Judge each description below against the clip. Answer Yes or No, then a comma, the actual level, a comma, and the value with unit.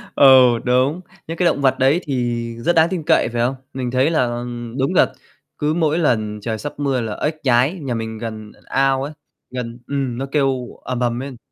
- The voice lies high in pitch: No, low, 130 Hz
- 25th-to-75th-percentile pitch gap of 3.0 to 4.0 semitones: Yes, average, 3.3 semitones